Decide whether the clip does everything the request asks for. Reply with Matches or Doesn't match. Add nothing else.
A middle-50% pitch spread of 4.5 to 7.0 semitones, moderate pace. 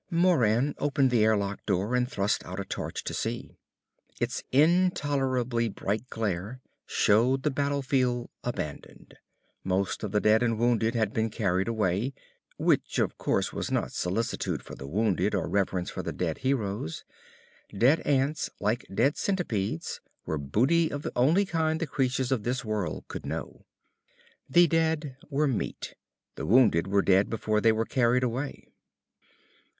Matches